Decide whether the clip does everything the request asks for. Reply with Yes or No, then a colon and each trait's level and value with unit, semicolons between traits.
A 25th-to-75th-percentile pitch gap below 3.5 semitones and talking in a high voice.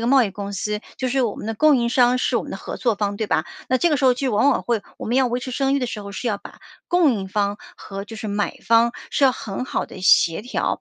No: average, 4.0 semitones; high, 235 Hz